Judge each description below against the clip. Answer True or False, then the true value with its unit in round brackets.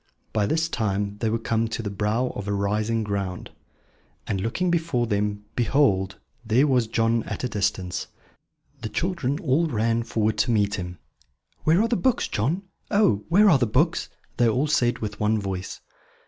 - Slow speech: False (175 wpm)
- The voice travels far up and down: False (4.8 semitones)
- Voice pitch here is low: True (115 Hz)